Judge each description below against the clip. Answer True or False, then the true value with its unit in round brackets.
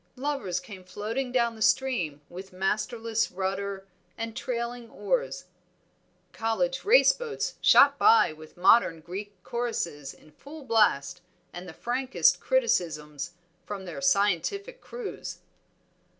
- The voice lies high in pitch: True (215 Hz)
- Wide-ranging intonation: True (6.3 semitones)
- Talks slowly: True (120 wpm)